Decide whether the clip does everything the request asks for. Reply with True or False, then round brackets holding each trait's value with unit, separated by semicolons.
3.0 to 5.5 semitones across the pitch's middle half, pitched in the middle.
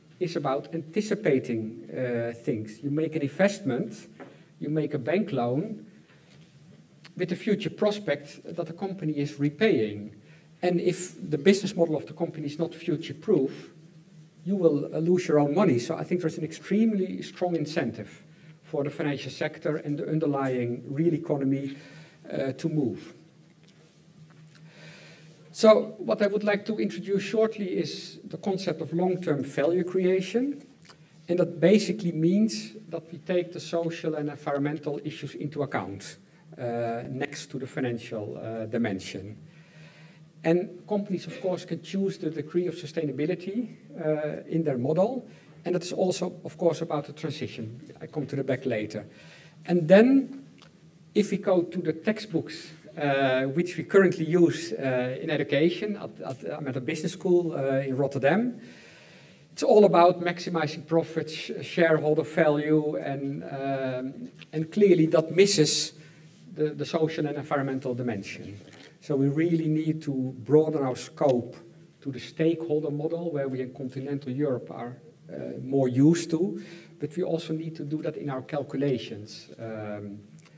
True (3.3 semitones; 160 Hz)